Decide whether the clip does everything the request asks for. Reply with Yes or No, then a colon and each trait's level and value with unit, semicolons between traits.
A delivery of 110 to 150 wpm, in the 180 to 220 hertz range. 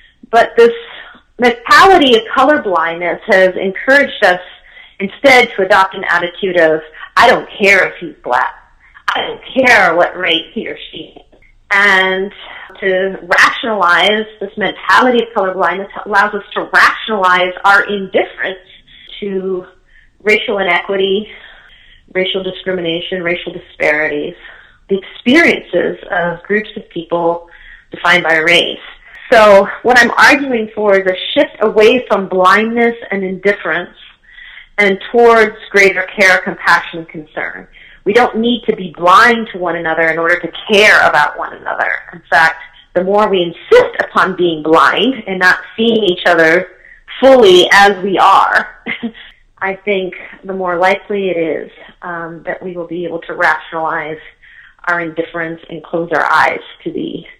Yes: average, 140 wpm; high, 190 Hz